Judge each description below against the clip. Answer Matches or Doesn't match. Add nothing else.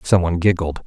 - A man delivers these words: Matches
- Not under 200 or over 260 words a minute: Matches